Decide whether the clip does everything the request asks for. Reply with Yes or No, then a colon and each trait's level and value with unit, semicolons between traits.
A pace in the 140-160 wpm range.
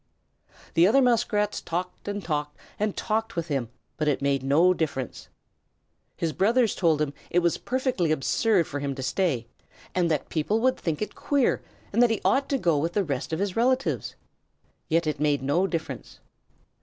No: average, 180 wpm